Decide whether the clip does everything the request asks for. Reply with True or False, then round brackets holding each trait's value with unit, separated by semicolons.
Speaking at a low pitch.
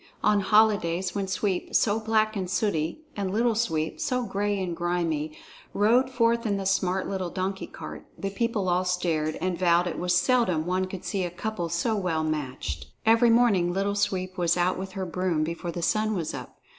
False (185 Hz)